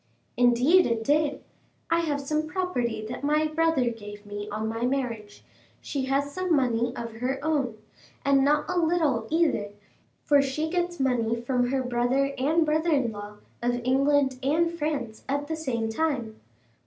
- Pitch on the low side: No, very high, 270 Hz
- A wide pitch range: No, average, 4.5 semitones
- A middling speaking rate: Yes, average, 165 wpm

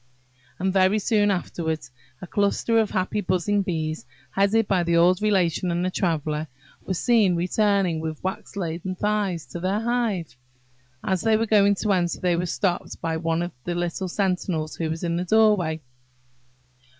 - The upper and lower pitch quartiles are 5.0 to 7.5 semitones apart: No, average, 3.2 semitones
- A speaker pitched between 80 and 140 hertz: No, medium, 185 Hz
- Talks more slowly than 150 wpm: No, average, 165 wpm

